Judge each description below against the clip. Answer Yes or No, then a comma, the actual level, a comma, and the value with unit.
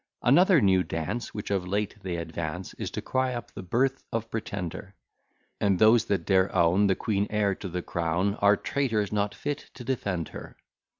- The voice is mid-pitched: No, low, 100 Hz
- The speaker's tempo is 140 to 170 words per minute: No, average, 185 wpm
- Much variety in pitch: No, average, 3.8 semitones